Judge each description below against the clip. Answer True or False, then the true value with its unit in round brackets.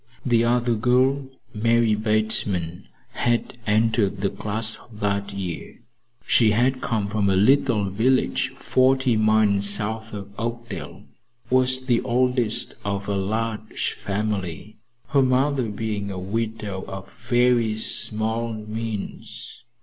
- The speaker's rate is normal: False (120 wpm)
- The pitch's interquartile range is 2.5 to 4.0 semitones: True (2.8 semitones)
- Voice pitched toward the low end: True (110 Hz)